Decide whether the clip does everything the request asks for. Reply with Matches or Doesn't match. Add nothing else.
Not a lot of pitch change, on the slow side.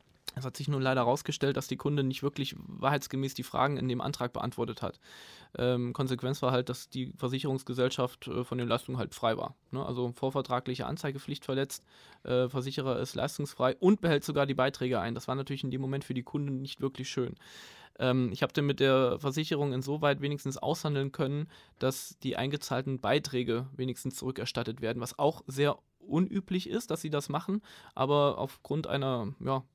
Doesn't match